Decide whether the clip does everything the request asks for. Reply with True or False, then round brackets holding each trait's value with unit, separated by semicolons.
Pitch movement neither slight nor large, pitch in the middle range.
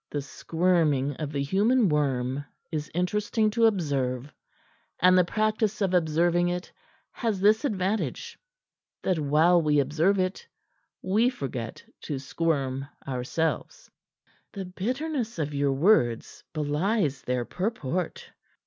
False (6.0 semitones; 170 Hz)